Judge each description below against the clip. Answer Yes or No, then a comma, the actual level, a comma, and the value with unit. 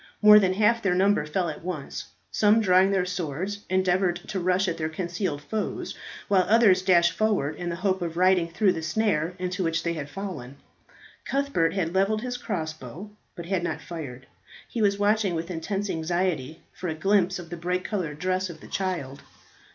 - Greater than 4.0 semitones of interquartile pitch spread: No, average, 3.2 semitones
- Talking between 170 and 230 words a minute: Yes, average, 190 wpm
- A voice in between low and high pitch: Yes, medium, 180 Hz